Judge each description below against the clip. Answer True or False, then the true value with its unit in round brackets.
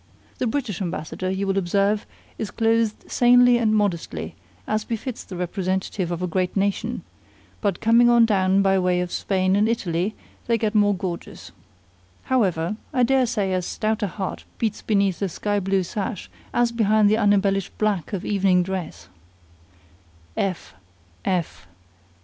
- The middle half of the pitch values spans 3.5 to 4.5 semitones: False (2.8 semitones)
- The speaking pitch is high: True (200 Hz)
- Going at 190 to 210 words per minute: False (150 wpm)